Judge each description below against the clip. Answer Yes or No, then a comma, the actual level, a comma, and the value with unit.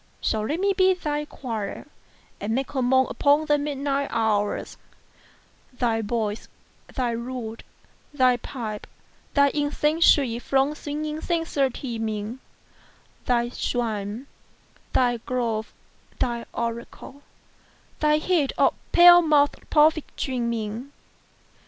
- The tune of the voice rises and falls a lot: No, average, 4.3 semitones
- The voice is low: No, very high, 255 Hz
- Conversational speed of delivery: No, slow, 115 wpm